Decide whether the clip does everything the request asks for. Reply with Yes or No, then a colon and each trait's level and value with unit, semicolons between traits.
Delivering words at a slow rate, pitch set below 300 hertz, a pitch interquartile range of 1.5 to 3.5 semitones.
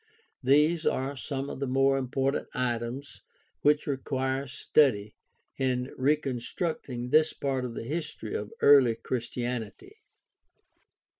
Yes: slow, 115 wpm; low, 135 Hz; narrow, 2.4 semitones